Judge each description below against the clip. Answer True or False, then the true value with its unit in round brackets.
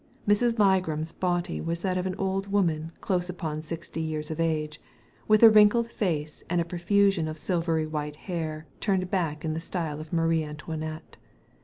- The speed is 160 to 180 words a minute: True (175 wpm)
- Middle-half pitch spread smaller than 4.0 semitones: True (3.3 semitones)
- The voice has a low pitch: False (165 Hz)